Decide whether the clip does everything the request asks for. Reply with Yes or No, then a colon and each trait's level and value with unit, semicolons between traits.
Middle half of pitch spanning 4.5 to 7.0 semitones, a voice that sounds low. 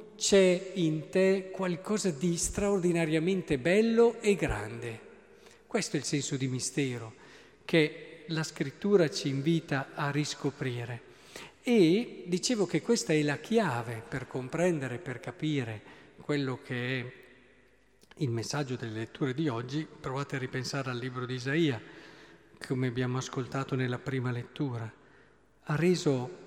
No: average, 5.3 semitones; medium, 145 Hz